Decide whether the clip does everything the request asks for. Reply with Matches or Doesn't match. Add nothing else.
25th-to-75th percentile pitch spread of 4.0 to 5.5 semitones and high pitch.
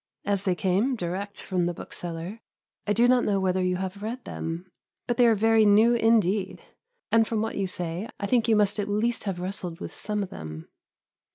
Doesn't match